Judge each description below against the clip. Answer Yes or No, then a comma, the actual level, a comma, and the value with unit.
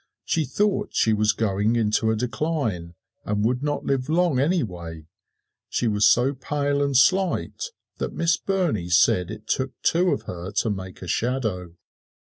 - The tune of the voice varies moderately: No, wide, 6.6 semitones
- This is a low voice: Yes, low, 120 Hz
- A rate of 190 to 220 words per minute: No, average, 160 wpm